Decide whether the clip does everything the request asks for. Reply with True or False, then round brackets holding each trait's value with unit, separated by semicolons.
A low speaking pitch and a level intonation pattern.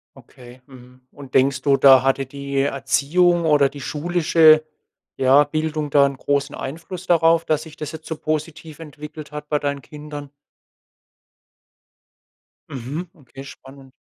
False (145 Hz; 2.3 semitones)